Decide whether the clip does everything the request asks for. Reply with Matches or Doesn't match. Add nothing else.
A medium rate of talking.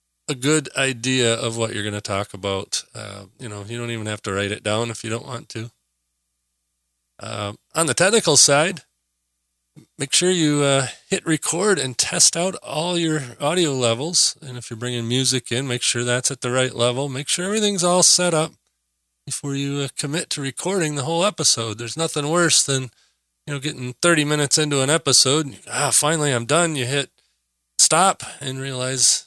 Matches